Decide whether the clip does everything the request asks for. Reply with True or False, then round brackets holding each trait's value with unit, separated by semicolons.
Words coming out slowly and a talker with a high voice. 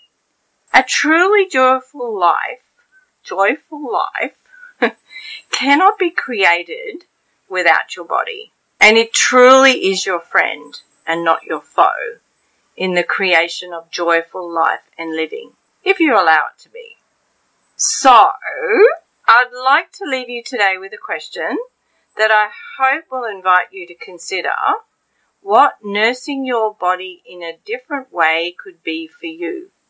True (130 wpm; 255 Hz)